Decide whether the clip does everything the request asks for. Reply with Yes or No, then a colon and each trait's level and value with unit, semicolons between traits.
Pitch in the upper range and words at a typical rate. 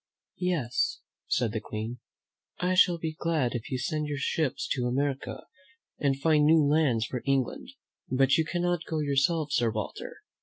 No: medium, 145 Hz; average, 160 wpm